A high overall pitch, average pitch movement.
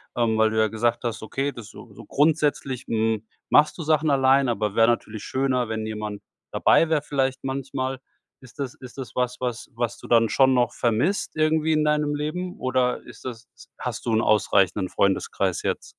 No: low, 125 Hz; average, 4.0 semitones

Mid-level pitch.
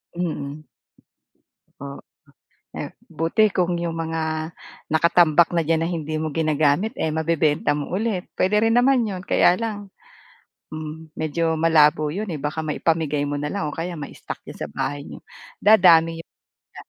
Yes: medium, 165 Hz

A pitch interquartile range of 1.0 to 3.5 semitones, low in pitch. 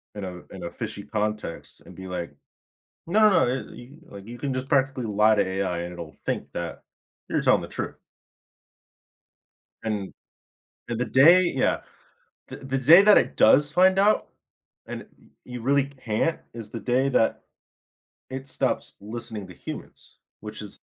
No: average, 4.9 semitones; low, 115 Hz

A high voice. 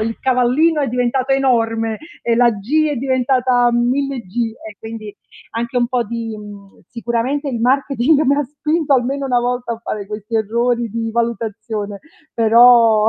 Yes: high, 240 Hz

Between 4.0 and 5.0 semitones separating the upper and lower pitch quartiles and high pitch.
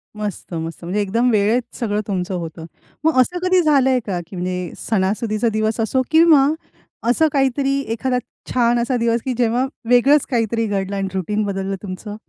Yes: average, 4.6 semitones; high, 225 Hz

